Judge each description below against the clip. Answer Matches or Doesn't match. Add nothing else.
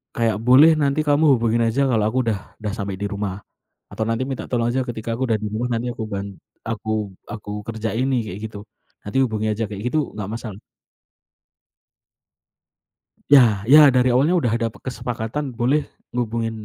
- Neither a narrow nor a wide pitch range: Matches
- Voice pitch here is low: Matches